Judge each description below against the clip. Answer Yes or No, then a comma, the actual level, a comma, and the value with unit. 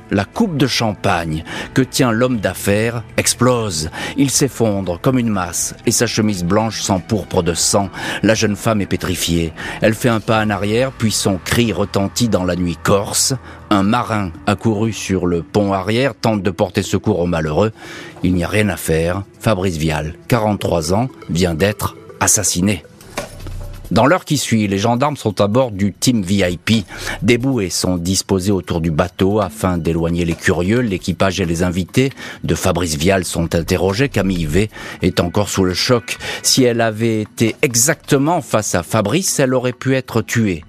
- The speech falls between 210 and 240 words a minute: No, average, 175 wpm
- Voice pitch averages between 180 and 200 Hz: No, low, 100 Hz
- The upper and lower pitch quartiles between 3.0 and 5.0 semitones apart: Yes, average, 4.2 semitones